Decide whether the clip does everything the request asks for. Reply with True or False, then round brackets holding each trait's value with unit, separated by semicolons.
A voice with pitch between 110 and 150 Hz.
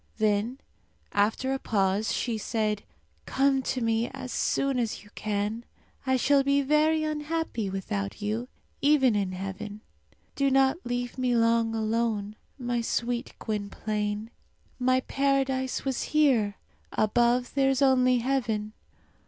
False (240 Hz)